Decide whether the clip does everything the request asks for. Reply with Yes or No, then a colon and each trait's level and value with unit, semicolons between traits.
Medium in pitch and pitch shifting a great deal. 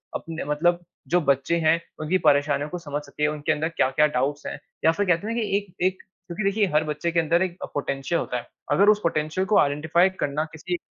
No: medium, 160 Hz; average, 3.3 semitones